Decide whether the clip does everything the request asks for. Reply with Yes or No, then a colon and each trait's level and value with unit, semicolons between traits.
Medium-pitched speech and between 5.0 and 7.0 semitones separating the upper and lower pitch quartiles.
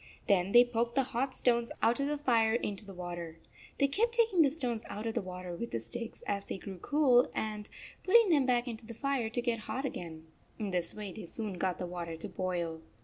No: high, 225 Hz; wide, 5.6 semitones